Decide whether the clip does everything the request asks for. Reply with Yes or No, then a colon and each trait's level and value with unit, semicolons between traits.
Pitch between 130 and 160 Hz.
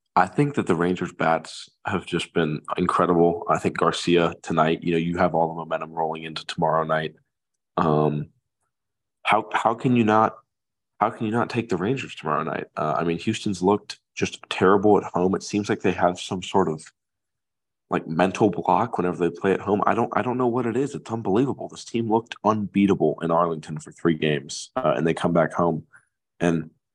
No: very low, 90 Hz